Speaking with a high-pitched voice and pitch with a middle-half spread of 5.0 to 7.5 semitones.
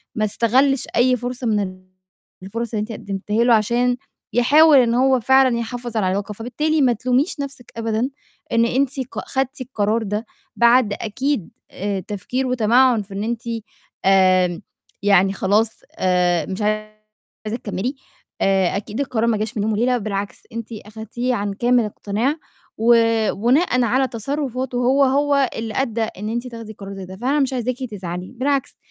No: high, 230 Hz; average, 3.5 semitones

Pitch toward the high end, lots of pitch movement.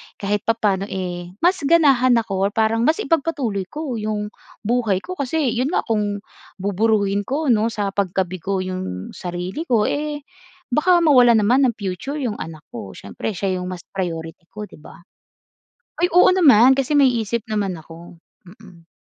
Yes: high, 210 Hz; wide, 5.8 semitones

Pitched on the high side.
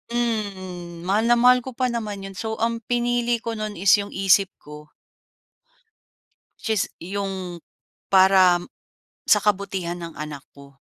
Yes: high, 195 Hz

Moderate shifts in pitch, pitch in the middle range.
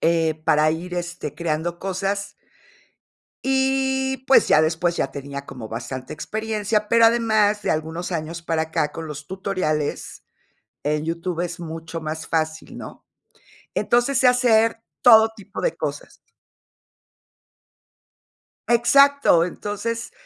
No: wide, 6.0 semitones; medium, 175 Hz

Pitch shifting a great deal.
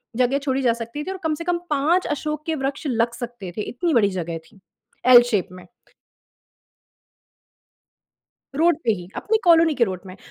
Yes: wide, 6.5 semitones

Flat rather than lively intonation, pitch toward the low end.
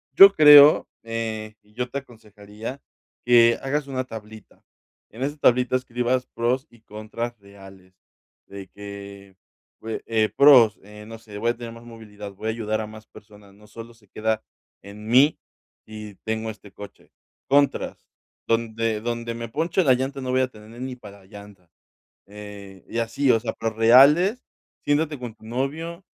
No: average, 3.2 semitones; low, 115 Hz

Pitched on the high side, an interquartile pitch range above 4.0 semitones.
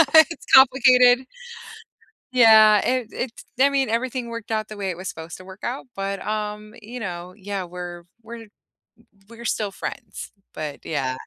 Yes: high, 215 Hz; average, 4.6 semitones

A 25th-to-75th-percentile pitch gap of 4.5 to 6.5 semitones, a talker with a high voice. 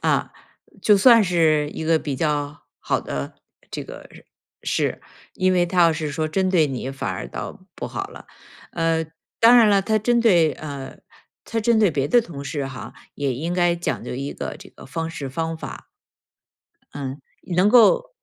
No: average, 5.2 semitones; medium, 165 Hz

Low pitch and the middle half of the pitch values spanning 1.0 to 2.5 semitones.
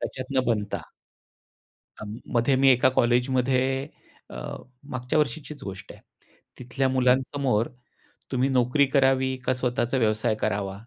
Yes: low, 130 Hz; narrow, 2.0 semitones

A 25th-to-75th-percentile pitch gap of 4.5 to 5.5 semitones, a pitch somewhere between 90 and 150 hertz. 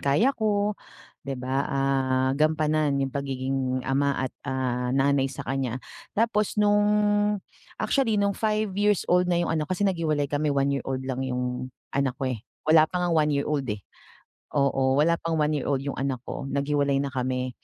No: average, 3.9 semitones; medium, 140 Hz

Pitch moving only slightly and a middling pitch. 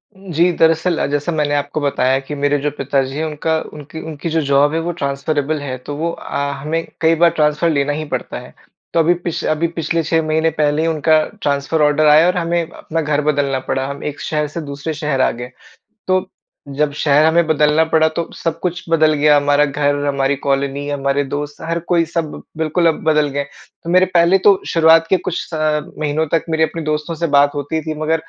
Yes: narrow, 2.3 semitones; medium, 155 Hz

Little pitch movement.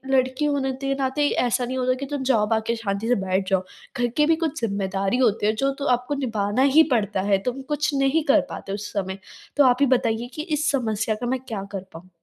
No: average, 4.8 semitones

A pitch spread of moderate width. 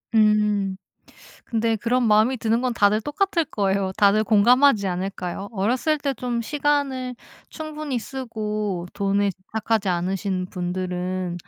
Yes: average, 4.5 semitones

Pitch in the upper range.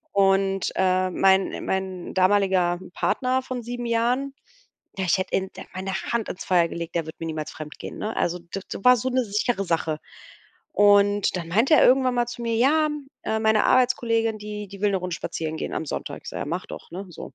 Yes: high, 200 Hz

